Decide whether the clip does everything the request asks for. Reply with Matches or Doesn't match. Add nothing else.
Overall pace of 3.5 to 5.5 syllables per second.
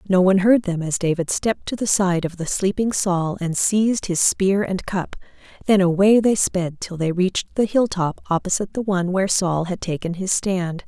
Matches